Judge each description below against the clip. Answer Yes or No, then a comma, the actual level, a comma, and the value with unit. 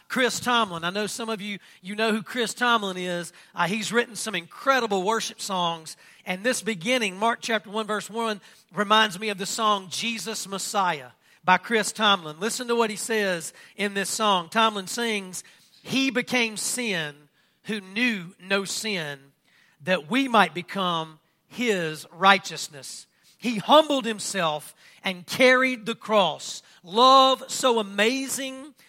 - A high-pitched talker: Yes, high, 210 Hz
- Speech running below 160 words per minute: Yes, average, 145 wpm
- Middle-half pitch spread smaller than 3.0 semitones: No, average, 4.0 semitones